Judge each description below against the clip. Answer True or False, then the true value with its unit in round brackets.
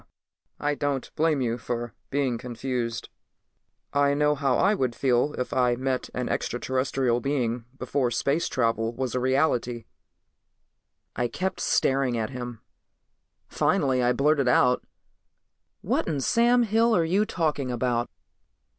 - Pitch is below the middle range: True (130 Hz)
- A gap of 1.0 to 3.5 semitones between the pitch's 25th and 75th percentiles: True (2.8 semitones)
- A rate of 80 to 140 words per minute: True (135 wpm)